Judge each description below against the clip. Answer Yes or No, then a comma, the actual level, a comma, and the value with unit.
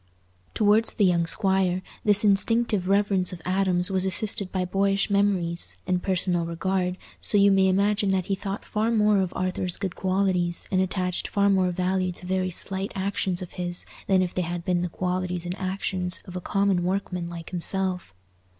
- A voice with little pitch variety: Yes, narrow, 1.6 semitones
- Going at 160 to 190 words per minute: Yes, average, 180 wpm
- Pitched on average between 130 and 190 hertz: Yes, medium, 185 Hz